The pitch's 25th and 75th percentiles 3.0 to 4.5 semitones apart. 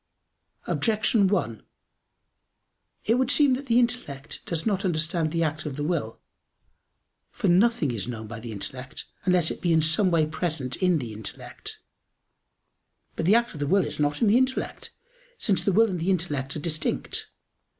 No: wide, 5.6 semitones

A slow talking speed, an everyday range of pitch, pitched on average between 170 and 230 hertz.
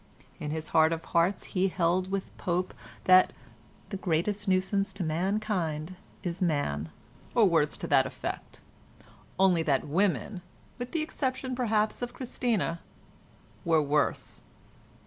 Yes: slow, 125 wpm; average, 4.3 semitones; medium, 185 Hz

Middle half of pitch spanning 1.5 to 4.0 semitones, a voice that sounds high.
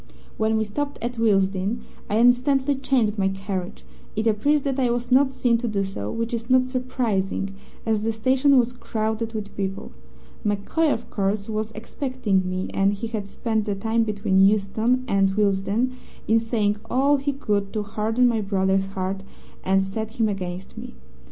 Yes: average, 3.7 semitones; high, 220 Hz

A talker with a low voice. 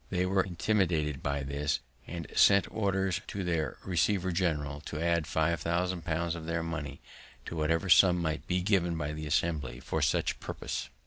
Yes: very low, 85 Hz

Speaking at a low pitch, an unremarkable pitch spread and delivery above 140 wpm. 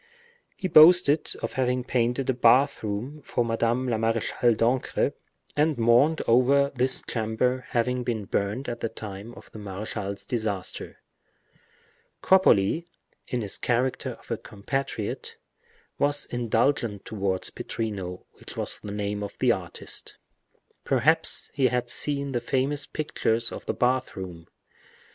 No: low, 120 Hz; average, 3.7 semitones; slow, 135 wpm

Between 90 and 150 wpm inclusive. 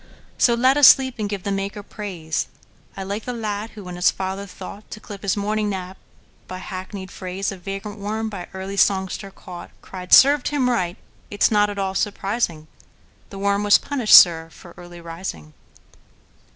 No: average, 165 wpm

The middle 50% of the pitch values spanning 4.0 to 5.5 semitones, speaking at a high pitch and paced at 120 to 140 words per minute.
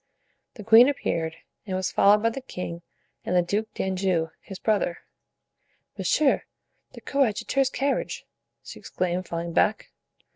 Yes: average, 4.4 semitones; high, 195 Hz; slow, 135 wpm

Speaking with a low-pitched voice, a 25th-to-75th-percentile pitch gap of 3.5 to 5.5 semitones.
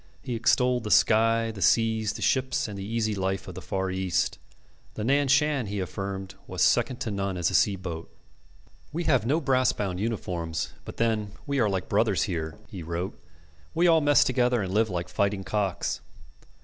Yes: low, 105 Hz; average, 4.4 semitones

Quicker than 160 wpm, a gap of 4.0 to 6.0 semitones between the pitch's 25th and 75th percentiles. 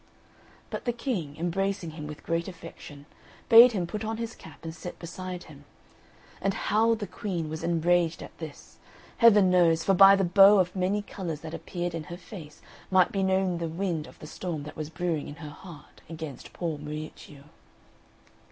No: average, 185 wpm; average, 3.5 semitones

